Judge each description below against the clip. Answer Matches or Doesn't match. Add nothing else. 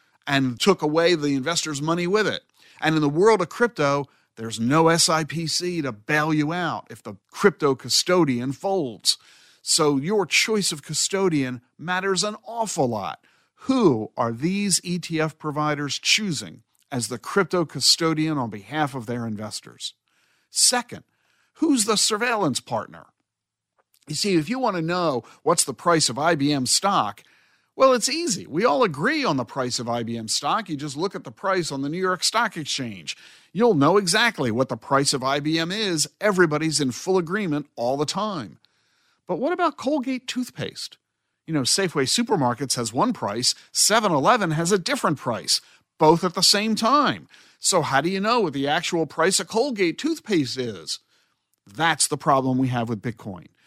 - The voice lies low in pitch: Doesn't match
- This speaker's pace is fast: Doesn't match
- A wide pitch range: Matches